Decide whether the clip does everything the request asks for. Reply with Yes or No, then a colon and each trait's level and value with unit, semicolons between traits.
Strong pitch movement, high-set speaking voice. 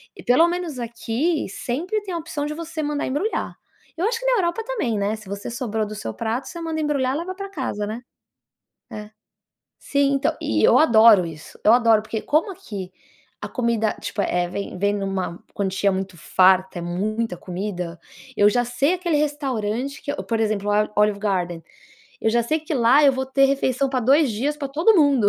Yes: wide, 6.4 semitones; high, 235 Hz